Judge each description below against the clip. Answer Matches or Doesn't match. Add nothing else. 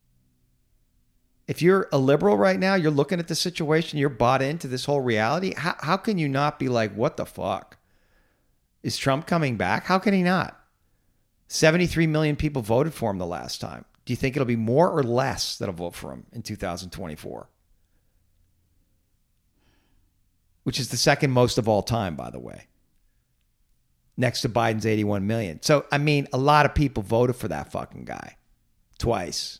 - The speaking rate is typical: Matches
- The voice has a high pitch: Doesn't match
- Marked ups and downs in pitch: Matches